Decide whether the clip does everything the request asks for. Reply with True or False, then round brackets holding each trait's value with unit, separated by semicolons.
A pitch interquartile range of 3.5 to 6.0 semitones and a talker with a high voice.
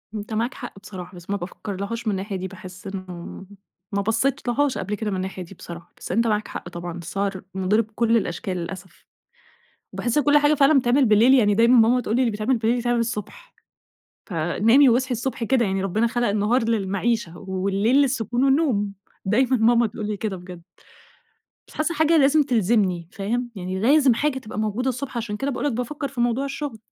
True (4.4 semitones; 225 Hz)